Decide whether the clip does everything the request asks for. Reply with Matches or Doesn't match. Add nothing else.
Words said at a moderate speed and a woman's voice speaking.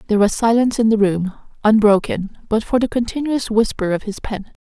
Matches